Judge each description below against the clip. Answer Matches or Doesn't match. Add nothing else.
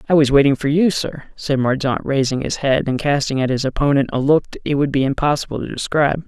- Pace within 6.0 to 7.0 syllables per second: Matches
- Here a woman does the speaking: Doesn't match